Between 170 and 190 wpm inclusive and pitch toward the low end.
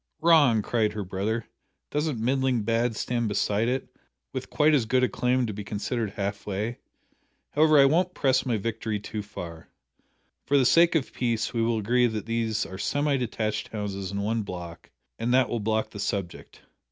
Yes: average, 185 wpm; low, 115 Hz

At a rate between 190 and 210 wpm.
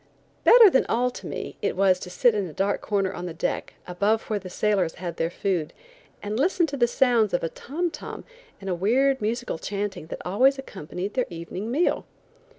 Yes: average, 200 wpm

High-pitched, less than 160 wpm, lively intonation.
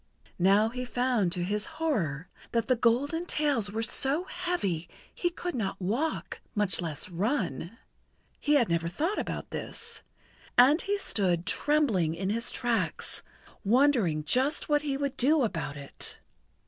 Yes: high, 230 Hz; average, 150 wpm; wide, 8.0 semitones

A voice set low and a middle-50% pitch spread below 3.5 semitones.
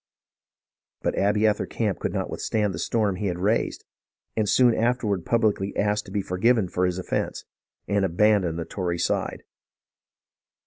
Yes: low, 100 Hz; average, 2.9 semitones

